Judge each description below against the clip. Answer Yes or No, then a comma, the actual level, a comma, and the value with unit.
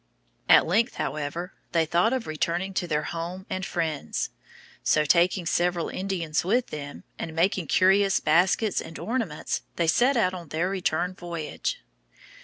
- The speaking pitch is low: No, medium, 175 Hz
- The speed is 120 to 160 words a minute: Yes, average, 150 wpm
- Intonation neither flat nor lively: Yes, average, 3.1 semitones